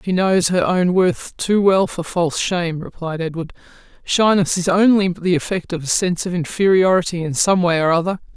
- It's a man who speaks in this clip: No, female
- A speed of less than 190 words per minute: No, average, 195 wpm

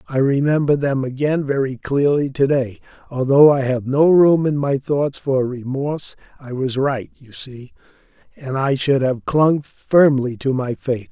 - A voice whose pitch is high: No, low, 135 Hz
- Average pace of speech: Yes, average, 175 wpm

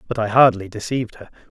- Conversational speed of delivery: Yes, average, 190 wpm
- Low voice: Yes, low, 110 Hz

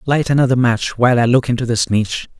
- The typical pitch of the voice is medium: No, low, 120 Hz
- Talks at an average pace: No, fast, 225 wpm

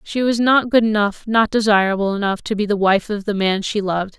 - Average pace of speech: No, fast, 245 wpm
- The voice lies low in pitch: No, high, 210 Hz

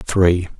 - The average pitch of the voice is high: No, very low, 85 Hz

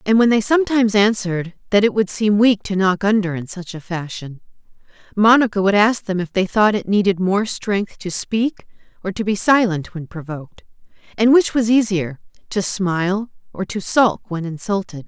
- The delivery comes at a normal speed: Yes, average, 185 wpm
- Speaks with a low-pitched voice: No, high, 200 Hz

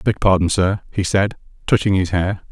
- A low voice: Yes, very low, 95 Hz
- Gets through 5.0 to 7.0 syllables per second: Yes, 5.1 syllables/s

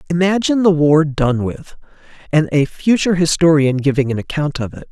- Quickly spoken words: No, average, 170 wpm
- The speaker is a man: Yes, male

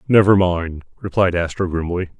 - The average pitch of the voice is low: Yes, very low, 90 Hz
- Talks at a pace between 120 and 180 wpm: Yes, slow, 135 wpm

